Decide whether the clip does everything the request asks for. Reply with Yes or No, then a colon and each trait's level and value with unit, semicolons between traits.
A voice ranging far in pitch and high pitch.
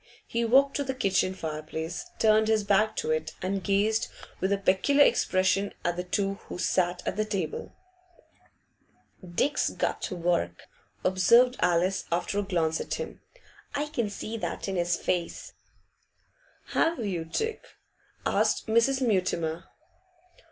No: average, 4.2 semitones; high, 195 Hz